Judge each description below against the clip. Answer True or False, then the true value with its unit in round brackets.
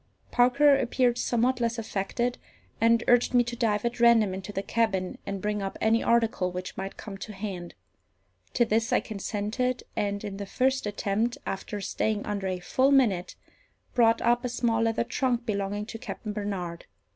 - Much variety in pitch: False (3.3 semitones)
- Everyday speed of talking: True (175 wpm)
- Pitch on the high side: True (220 Hz)